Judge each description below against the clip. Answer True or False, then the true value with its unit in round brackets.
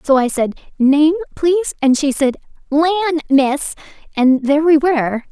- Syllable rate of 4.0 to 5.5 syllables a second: True (5.0 syllables/s)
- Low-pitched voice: False (295 Hz)